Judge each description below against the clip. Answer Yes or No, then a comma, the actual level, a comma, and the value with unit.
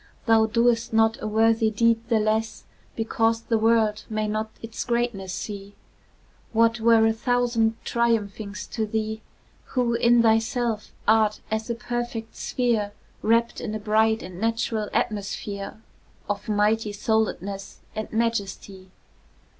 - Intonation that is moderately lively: No, narrow, 1.4 semitones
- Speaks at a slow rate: Yes, slow, 130 wpm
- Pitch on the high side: Yes, high, 220 Hz